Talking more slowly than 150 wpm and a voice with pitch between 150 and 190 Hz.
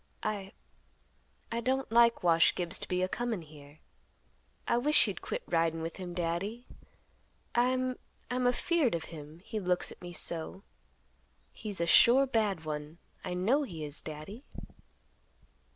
Yes: slow, 135 wpm; medium, 185 Hz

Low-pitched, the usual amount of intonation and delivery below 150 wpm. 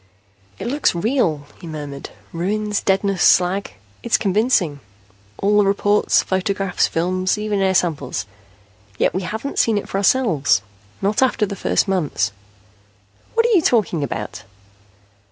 No: high, 195 Hz; average, 4.2 semitones; average, 140 wpm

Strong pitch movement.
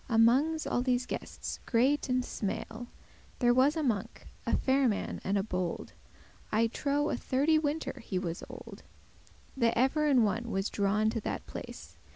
No: average, 4.3 semitones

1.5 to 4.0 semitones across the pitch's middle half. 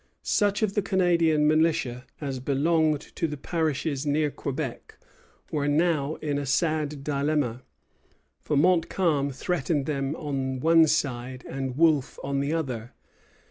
Yes: average, 2.9 semitones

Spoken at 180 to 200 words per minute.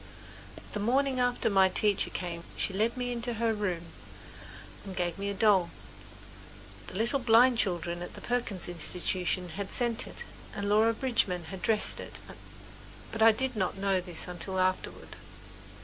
No: average, 160 wpm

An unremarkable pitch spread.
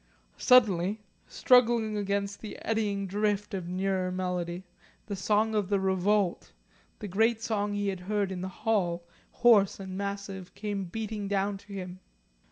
No: narrow, 2.0 semitones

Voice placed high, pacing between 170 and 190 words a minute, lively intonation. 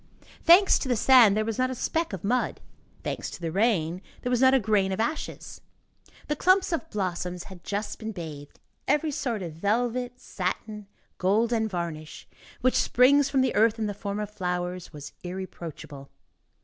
Yes: high, 210 Hz; average, 180 wpm; wide, 5.7 semitones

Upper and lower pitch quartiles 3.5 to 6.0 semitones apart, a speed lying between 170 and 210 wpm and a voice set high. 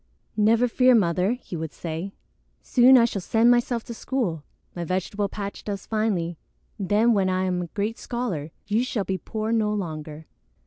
Yes: average, 4.5 semitones; average, 175 wpm; high, 205 Hz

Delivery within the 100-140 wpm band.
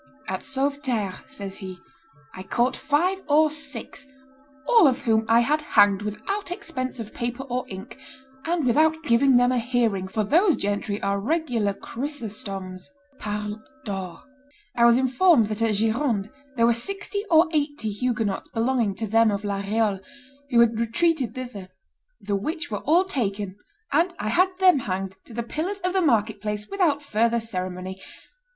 No: average, 160 wpm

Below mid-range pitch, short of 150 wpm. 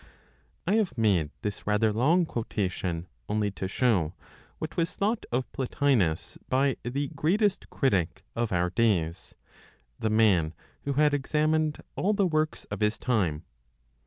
Yes: low, 115 Hz; average, 140 wpm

